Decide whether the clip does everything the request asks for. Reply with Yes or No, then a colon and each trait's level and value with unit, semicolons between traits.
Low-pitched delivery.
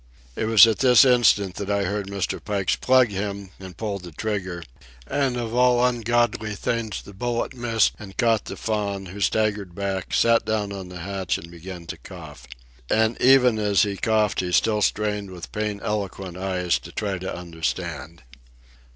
Yes: low, 100 Hz